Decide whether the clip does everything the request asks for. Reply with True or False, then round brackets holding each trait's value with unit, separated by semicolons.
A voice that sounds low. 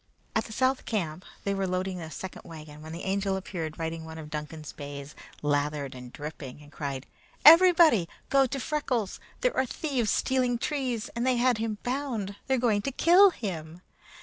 False (195 Hz)